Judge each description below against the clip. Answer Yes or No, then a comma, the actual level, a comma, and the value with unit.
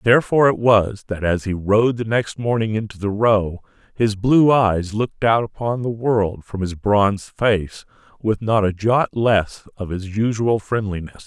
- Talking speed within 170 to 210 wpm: Yes, average, 180 wpm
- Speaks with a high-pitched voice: No, low, 105 Hz